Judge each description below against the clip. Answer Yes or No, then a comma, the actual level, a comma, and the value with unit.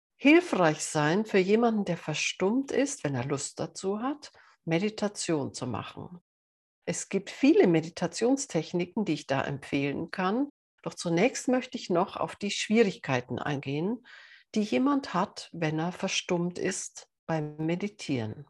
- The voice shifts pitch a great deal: Yes, wide, 6.1 semitones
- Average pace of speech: Yes, average, 135 wpm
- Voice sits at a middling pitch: Yes, medium, 175 Hz